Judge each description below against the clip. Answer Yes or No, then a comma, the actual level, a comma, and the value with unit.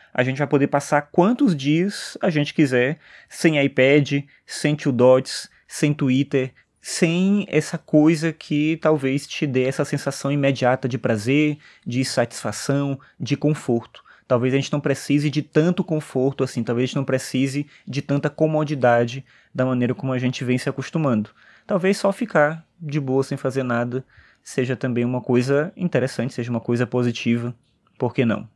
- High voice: No, medium, 140 Hz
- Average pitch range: Yes, average, 3.0 semitones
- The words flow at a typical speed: Yes, average, 160 wpm